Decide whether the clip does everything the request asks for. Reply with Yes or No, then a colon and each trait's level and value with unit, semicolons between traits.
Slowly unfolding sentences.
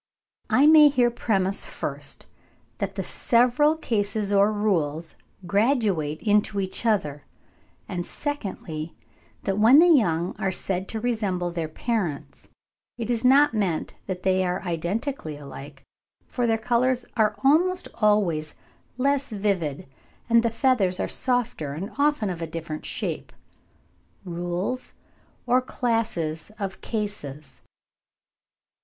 Yes: slow, 125 wpm